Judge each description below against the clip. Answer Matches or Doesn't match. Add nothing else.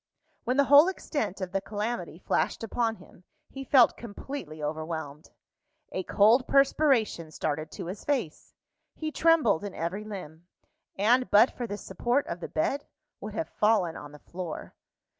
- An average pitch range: Doesn't match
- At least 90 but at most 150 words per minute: Doesn't match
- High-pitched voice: Matches